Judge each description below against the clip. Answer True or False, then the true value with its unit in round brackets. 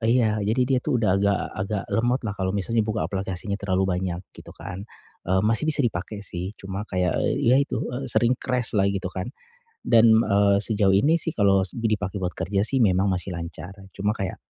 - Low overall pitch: True (100 Hz)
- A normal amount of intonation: True (3.1 semitones)